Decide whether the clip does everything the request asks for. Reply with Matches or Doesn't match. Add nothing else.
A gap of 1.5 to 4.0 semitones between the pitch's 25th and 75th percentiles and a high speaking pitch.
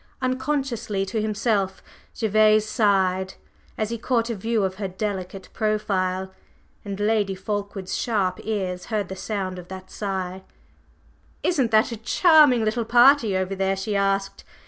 Matches